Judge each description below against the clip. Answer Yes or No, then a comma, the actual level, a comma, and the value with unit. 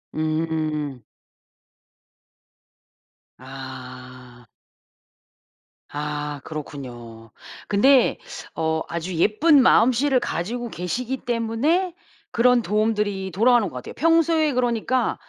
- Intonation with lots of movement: Yes, wide, 9.0 semitones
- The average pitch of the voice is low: No, high, 195 Hz